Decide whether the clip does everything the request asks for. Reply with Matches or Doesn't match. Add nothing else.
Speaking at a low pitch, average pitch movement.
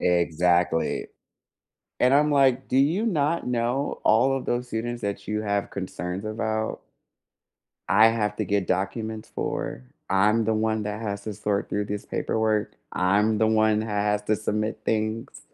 Doesn't match